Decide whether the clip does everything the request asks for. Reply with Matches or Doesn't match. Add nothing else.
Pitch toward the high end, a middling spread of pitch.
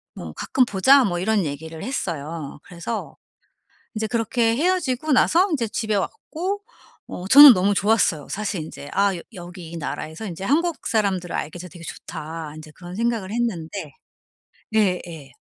Doesn't match